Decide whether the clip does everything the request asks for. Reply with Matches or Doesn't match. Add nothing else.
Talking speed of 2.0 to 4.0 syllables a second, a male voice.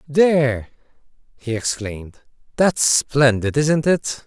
Matches